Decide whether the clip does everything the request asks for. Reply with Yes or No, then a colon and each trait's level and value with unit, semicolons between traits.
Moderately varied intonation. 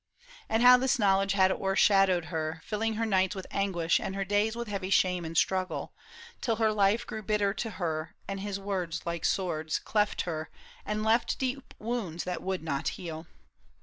Yes: average, 3.5 semitones